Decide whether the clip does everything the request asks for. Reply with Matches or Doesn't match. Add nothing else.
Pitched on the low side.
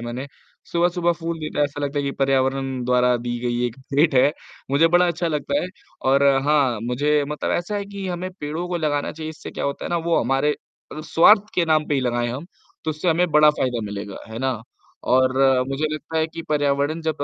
Doesn't match